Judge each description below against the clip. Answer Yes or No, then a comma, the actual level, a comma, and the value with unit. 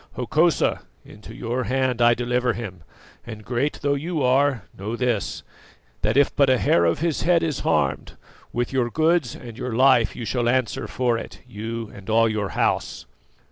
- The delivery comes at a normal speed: Yes, average, 180 wpm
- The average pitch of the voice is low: Yes, low, 120 Hz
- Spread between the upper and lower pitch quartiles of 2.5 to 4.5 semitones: Yes, average, 2.9 semitones